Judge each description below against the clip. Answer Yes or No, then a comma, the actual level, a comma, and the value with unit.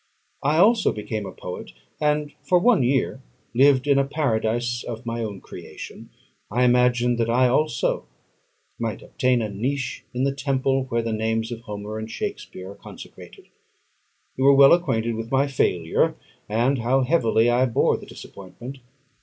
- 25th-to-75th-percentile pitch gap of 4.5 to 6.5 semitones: No, average, 3.4 semitones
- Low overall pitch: Yes, low, 125 Hz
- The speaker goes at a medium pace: Yes, average, 160 wpm